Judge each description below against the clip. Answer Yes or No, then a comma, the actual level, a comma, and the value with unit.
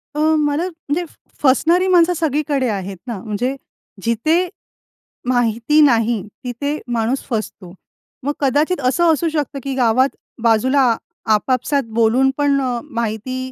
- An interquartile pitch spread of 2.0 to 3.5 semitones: No, average, 4.3 semitones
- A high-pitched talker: Yes, very high, 260 Hz